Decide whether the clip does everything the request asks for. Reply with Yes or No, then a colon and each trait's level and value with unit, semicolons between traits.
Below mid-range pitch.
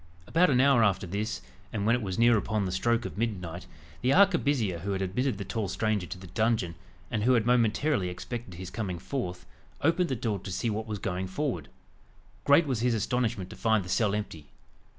Yes: low, 110 Hz